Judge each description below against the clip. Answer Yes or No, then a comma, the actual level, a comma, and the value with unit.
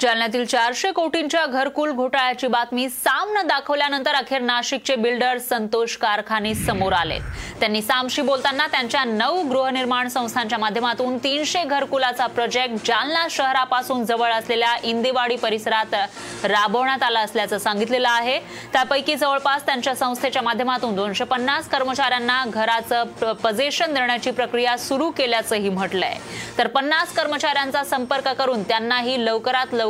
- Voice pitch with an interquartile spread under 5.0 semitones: Yes, average, 2.9 semitones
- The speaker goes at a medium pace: Yes, average, 110 wpm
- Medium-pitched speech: No, very high, 255 Hz